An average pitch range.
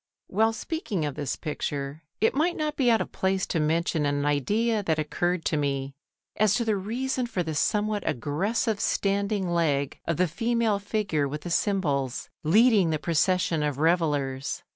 No: wide, 6.4 semitones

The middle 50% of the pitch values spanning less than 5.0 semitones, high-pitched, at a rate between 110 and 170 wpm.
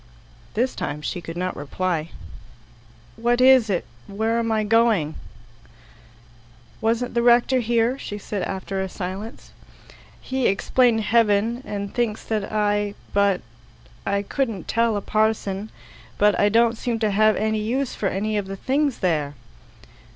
Yes: average, 2.9 semitones; high, 215 Hz; average, 145 wpm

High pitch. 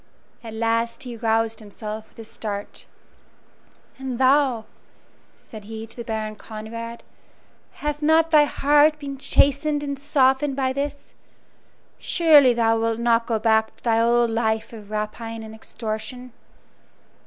Yes: high, 230 Hz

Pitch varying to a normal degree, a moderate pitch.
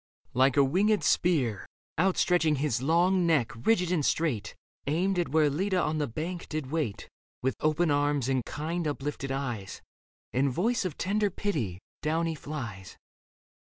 Yes: average, 4.6 semitones; medium, 155 Hz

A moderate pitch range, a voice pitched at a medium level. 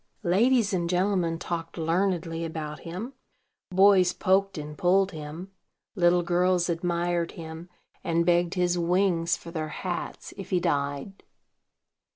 No: narrow, 2.0 semitones; medium, 175 Hz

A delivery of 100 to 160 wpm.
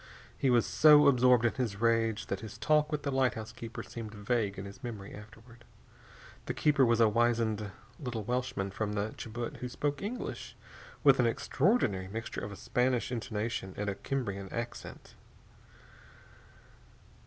Yes: average, 155 wpm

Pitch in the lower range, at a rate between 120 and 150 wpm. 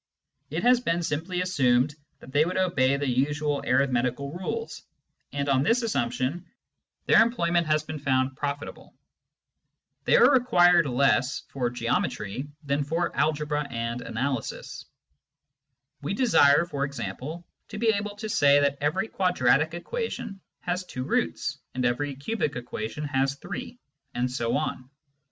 No: medium, 145 Hz; average, 140 wpm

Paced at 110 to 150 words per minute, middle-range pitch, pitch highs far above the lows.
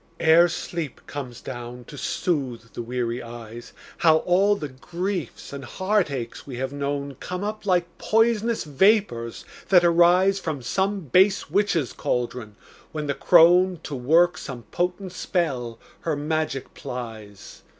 Yes: average, 140 wpm; medium, 155 Hz; wide, 6.5 semitones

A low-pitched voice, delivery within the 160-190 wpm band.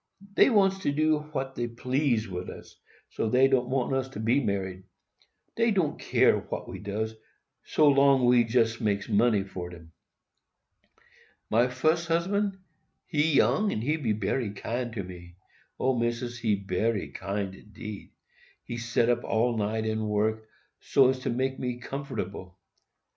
No: low, 120 Hz; average, 150 wpm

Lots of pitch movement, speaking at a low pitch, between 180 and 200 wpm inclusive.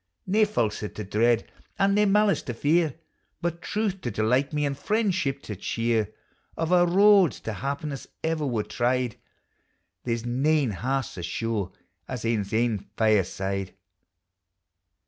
No: wide, 7.5 semitones; low, 130 Hz; average, 145 wpm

